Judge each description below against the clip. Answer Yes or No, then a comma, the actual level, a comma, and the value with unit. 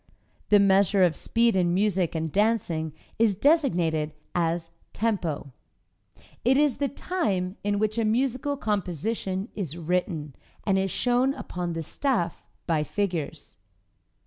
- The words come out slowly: Yes, slow, 130 wpm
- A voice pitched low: No, high, 195 Hz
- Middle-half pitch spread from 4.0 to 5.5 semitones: Yes, average, 5.2 semitones